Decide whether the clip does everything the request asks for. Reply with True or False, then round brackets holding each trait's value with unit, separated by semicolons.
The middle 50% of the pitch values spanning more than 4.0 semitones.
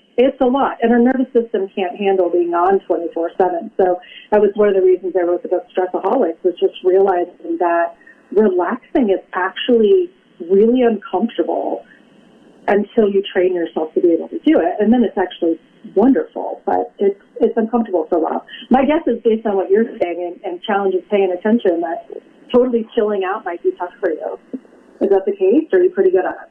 True (5.2 semitones)